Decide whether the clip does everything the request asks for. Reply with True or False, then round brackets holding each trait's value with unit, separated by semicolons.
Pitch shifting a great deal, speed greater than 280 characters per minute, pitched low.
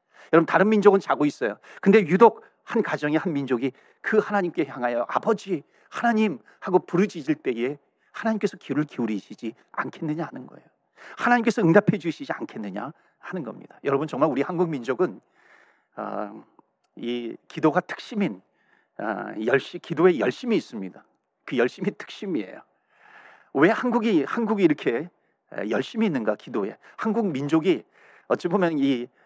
False (7.0 semitones; 325 characters per minute; 180 Hz)